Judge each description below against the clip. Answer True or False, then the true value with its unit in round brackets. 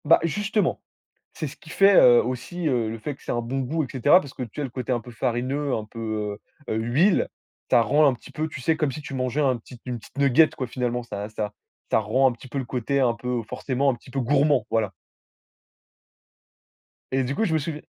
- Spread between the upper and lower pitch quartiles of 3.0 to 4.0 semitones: True (3.7 semitones)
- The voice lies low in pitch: True (130 Hz)